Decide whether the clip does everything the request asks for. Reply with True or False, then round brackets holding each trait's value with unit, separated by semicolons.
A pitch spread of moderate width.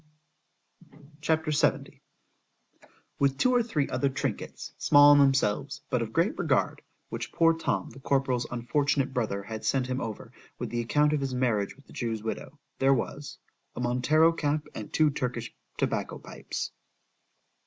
True (3.4 semitones)